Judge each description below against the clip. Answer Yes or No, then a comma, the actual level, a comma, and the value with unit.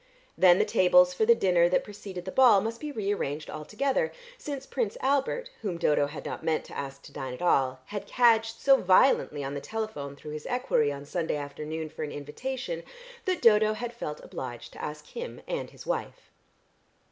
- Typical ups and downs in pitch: No, wide, 8.1 semitones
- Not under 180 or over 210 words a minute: Yes, average, 195 wpm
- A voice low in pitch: No, medium, 185 Hz